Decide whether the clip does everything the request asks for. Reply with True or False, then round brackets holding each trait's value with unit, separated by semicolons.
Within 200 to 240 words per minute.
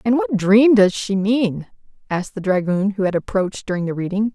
True (205 wpm)